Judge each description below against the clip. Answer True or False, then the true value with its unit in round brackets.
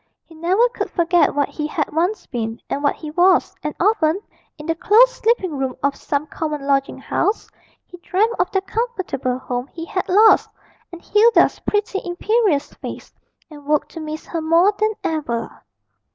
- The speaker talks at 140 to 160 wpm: False (175 wpm)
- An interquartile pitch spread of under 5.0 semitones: False (5.3 semitones)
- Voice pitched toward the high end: True (330 Hz)